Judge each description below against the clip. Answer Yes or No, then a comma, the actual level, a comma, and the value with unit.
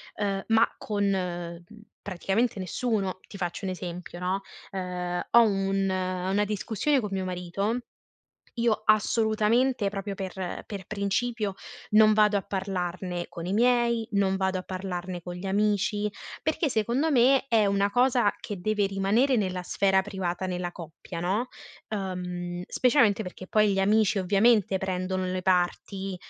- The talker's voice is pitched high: Yes, high, 195 Hz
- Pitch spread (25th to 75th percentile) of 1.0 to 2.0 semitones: No, narrow, 2.6 semitones